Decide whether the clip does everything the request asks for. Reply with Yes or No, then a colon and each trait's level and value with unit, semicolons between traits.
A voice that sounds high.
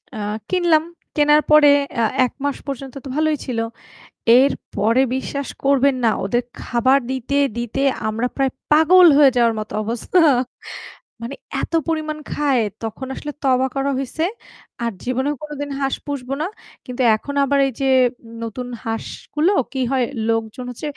Yes: very high, 270 Hz